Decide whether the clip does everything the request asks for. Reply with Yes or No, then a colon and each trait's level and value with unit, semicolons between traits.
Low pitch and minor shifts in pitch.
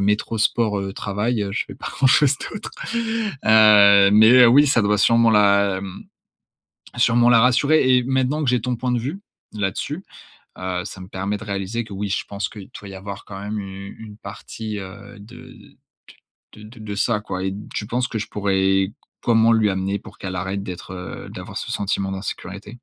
No: low, 105 Hz; average, 3.2 semitones